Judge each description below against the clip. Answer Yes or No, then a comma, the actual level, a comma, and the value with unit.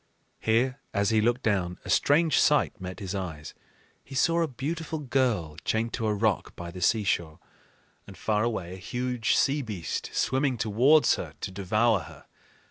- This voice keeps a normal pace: Yes, average, 170 wpm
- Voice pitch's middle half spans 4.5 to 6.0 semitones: Yes, wide, 5.5 semitones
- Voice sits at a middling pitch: No, low, 110 Hz